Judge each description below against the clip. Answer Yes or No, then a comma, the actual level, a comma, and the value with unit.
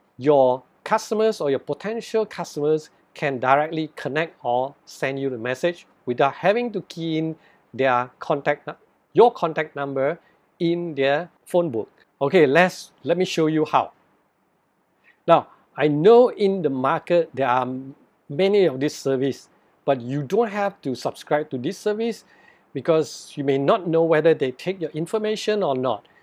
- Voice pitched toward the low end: No, medium, 155 Hz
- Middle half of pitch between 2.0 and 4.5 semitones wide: No, average, 5.0 semitones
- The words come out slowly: No, average, 155 wpm